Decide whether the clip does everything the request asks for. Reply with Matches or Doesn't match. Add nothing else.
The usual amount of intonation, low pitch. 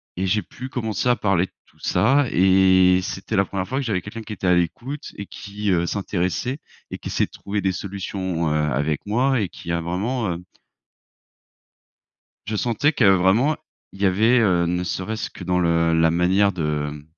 Matches